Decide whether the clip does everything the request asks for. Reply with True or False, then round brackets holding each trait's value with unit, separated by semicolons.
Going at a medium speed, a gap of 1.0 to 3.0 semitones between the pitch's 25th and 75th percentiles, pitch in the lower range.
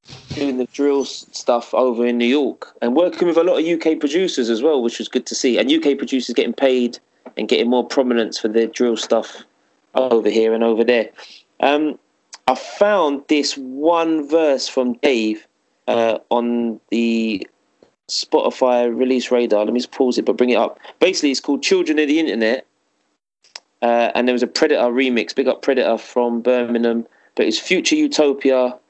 False (180 wpm; 3.5 semitones; 125 Hz)